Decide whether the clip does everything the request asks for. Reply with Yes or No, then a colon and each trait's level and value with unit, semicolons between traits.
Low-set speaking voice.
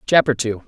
Yes: low, 125 Hz